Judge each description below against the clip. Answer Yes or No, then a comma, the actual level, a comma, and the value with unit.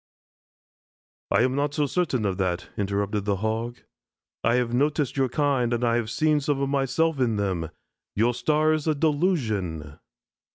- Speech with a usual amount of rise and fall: No, wide, 5.8 semitones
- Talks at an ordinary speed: Yes, average, 165 wpm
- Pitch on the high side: No, low, 125 Hz